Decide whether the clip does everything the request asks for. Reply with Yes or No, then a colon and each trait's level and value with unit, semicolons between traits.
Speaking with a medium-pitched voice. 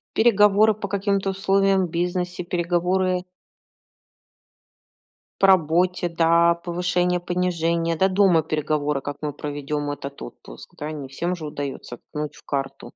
Yes: medium, 175 Hz